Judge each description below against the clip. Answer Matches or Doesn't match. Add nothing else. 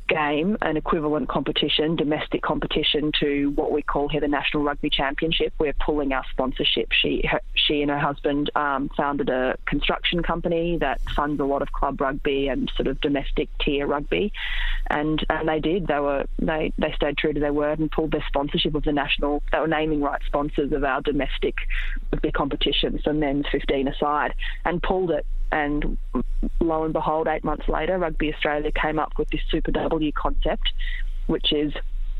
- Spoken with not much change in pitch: Matches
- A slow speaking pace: Doesn't match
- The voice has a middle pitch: Matches